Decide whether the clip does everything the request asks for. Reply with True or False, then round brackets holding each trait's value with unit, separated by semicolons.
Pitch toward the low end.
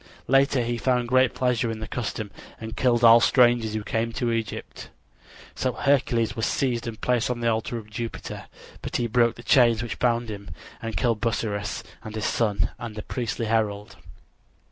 True (115 Hz)